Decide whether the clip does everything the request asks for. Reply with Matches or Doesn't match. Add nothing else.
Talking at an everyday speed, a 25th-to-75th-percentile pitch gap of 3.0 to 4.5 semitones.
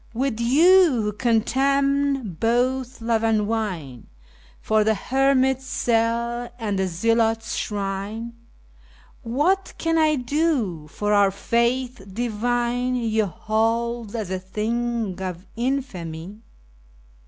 Doesn't match